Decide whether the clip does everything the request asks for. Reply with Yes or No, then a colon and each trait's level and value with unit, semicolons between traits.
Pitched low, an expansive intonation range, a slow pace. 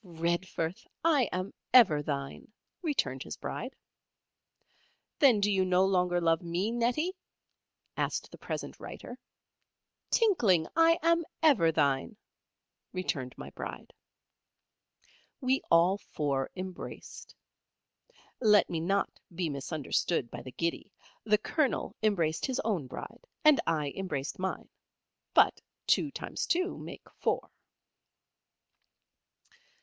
No: medium, 185 Hz; wide, 6.7 semitones; slow, 115 wpm